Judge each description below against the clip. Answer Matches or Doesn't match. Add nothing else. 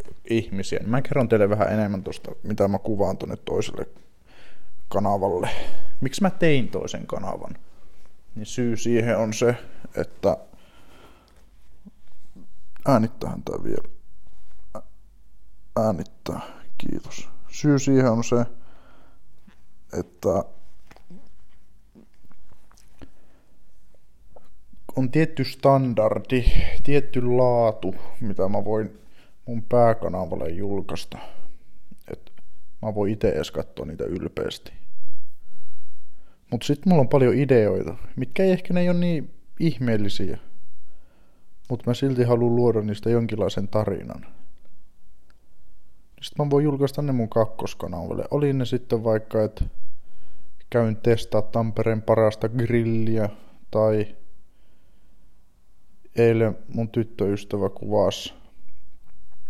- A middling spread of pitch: Matches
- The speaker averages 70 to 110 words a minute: Matches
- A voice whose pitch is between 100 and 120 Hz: Matches